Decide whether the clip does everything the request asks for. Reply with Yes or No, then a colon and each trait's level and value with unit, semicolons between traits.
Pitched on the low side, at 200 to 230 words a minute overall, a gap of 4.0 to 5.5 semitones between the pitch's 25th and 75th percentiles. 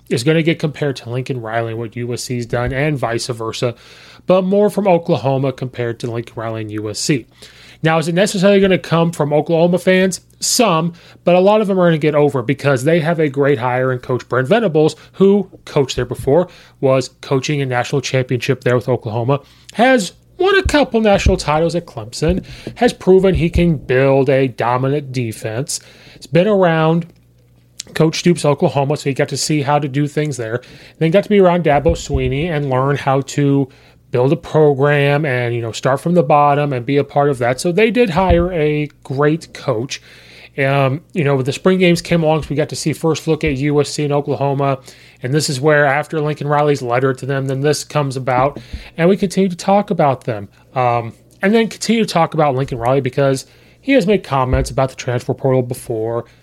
No: medium, 145 Hz; fast, 205 wpm; average, 4.6 semitones